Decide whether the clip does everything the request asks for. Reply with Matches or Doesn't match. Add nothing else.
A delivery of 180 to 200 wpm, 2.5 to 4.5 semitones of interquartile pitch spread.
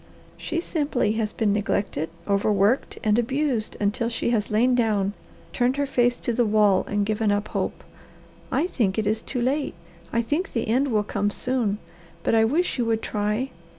Matches